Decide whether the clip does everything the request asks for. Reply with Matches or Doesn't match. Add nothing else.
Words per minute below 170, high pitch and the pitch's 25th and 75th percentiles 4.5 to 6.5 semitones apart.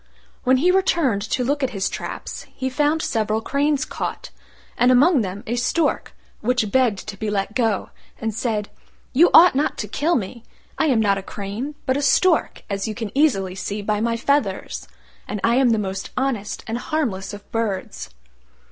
Doesn't match